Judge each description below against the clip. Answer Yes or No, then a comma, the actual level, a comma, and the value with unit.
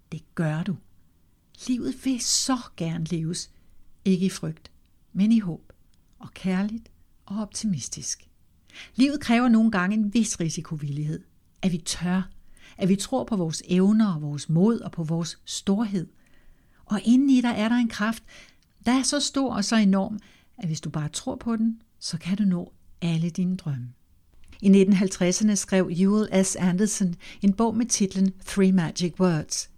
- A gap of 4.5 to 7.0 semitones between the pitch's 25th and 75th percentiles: Yes, average, 5.0 semitones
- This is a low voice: No, high, 190 Hz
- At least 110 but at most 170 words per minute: Yes, average, 165 wpm